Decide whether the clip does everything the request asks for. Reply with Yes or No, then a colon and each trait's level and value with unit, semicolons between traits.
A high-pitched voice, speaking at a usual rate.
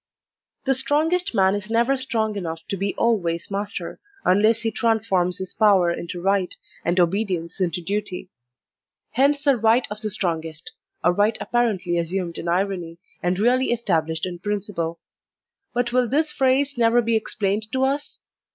Yes: high, 205 Hz; average, 165 wpm